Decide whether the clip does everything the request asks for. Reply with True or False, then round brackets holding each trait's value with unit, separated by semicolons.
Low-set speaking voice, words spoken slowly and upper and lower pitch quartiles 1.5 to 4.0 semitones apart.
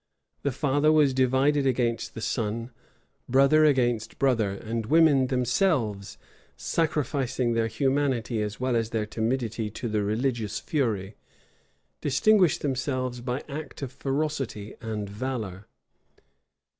True (125 Hz; 120 wpm; 3.7 semitones)